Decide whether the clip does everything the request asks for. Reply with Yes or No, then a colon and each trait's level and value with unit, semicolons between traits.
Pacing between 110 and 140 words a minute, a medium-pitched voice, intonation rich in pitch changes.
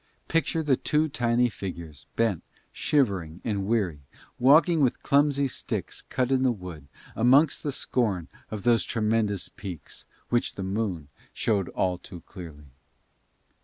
No: slow, 135 wpm; low, 110 Hz; wide, 6.3 semitones